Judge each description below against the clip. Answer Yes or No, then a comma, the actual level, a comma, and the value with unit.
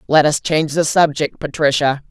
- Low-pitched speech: No, medium, 150 Hz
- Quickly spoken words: No, average, 170 wpm